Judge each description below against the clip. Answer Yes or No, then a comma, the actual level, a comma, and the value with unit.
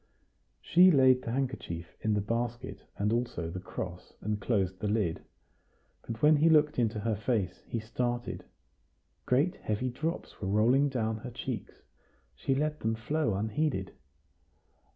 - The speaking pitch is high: No, low, 115 Hz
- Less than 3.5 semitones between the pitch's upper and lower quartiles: No, average, 4.2 semitones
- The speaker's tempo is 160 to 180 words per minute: No, average, 150 wpm